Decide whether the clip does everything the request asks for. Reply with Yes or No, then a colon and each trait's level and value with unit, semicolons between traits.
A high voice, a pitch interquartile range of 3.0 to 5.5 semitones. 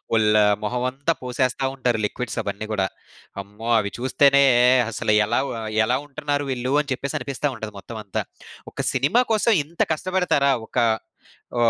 No: low, 130 Hz; average, 4.3 semitones